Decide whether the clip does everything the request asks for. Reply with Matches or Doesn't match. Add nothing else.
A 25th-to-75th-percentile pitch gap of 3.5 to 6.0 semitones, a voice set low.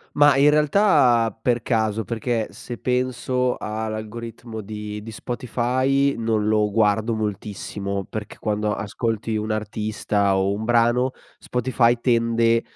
Doesn't match